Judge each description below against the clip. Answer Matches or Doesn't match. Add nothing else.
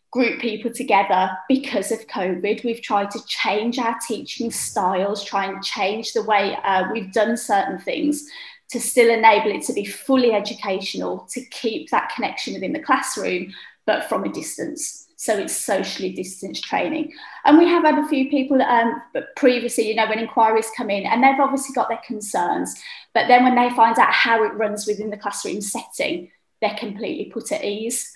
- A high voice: Matches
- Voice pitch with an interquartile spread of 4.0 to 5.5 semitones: Doesn't match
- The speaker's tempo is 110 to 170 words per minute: Doesn't match